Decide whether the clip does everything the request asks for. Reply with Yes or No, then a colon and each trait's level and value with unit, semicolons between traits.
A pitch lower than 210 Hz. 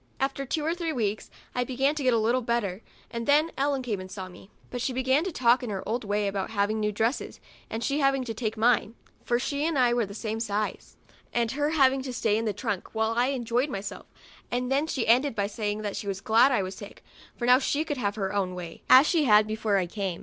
No: high, 235 Hz